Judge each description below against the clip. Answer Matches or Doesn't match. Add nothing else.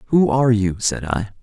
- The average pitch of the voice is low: Matches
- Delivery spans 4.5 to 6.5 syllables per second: Matches